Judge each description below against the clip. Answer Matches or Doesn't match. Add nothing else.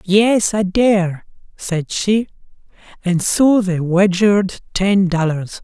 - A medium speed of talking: Doesn't match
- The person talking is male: Matches